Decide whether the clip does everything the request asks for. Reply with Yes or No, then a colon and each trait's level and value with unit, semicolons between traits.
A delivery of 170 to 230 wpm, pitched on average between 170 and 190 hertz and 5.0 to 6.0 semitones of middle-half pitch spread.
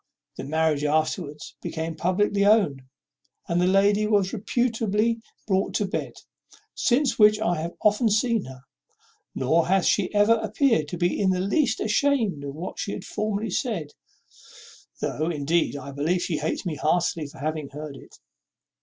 No: average, 160 wpm; medium, 185 Hz; wide, 5.4 semitones